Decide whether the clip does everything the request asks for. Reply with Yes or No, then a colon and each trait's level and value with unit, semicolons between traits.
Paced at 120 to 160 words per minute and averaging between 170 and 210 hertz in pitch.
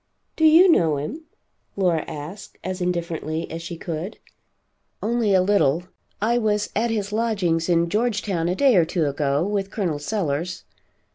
Yes: average, 155 wpm; medium, 185 Hz